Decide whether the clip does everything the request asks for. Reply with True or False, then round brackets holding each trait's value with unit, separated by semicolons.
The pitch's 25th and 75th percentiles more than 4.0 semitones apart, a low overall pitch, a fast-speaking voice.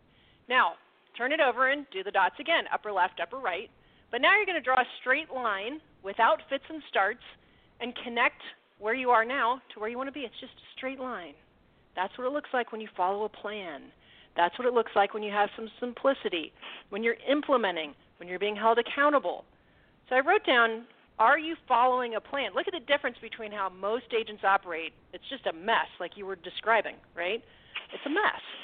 False (4.8 semitones; 235 Hz; 210 wpm)